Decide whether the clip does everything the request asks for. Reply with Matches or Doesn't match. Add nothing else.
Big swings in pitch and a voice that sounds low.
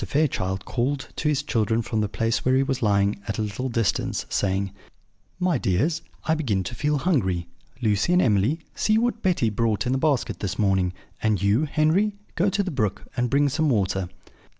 Matches